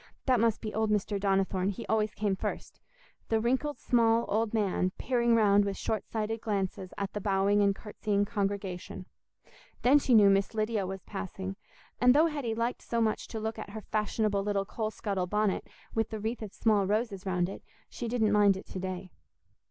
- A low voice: No, high, 210 Hz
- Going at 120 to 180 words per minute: No, average, 190 wpm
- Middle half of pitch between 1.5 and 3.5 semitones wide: Yes, narrow, 2.4 semitones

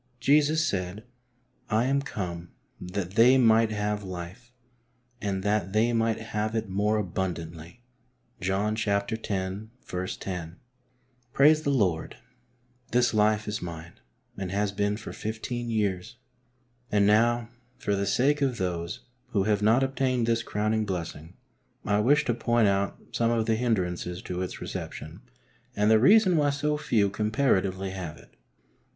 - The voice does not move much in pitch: No, average, 3.8 semitones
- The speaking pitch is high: No, low, 105 Hz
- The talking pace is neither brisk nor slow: Yes, average, 145 wpm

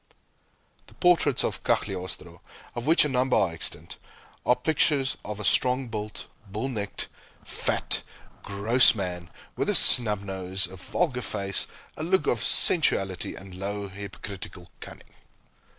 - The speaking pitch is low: Yes, low, 105 Hz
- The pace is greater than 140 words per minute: No, slow, 135 wpm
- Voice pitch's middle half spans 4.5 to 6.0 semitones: Yes, average, 5.0 semitones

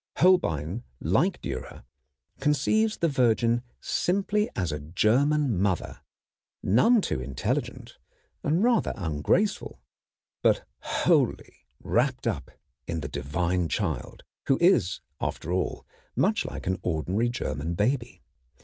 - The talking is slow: Yes, slow, 115 wpm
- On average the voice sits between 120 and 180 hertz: No, low, 110 Hz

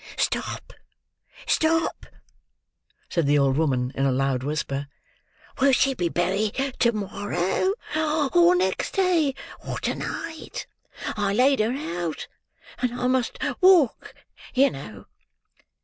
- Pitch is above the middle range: Yes, high, 210 Hz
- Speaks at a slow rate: Yes, slow, 120 wpm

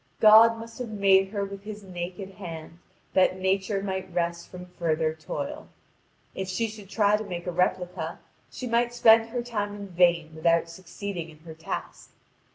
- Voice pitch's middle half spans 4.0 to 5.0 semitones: No, average, 3.6 semitones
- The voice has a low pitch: No, high, 190 Hz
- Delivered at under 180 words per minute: Yes, average, 170 wpm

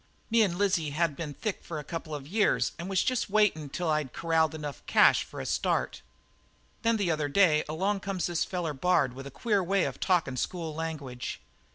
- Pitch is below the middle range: No, medium, 165 Hz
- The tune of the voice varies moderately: Yes, average, 4.2 semitones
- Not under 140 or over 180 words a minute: No, fast, 205 wpm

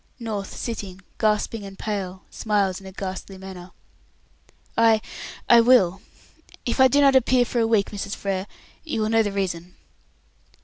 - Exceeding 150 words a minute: Yes, average, 160 wpm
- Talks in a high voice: Yes, high, 205 Hz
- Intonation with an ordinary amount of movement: Yes, average, 3.1 semitones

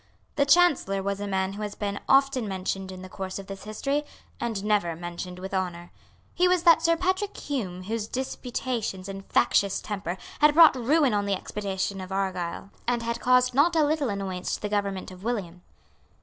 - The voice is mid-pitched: No, high, 205 Hz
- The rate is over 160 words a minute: Yes, average, 190 wpm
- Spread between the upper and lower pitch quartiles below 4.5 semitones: No, wide, 5.6 semitones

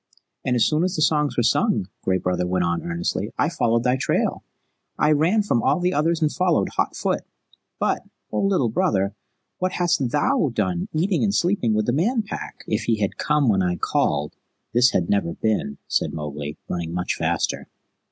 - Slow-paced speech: No, average, 190 wpm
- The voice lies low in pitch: Yes, low, 120 Hz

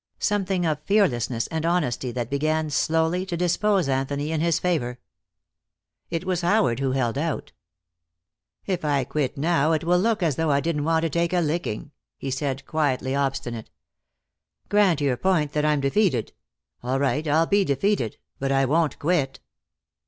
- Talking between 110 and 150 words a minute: No, average, 165 wpm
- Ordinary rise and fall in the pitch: Yes, average, 4.1 semitones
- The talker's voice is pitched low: No, medium, 155 Hz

